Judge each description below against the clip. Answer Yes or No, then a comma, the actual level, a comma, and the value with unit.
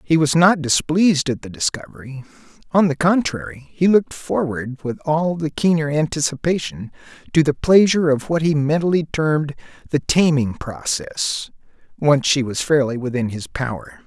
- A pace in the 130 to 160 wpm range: Yes, average, 155 wpm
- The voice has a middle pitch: Yes, medium, 150 Hz